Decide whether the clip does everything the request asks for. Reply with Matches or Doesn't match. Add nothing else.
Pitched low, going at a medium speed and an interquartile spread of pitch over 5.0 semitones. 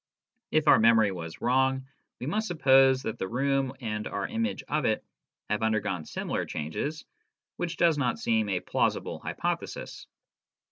Matches